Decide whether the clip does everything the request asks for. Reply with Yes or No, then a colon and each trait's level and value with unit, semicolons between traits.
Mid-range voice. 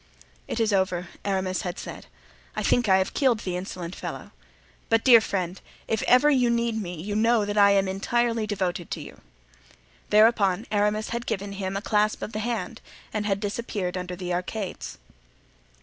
No: high, 205 Hz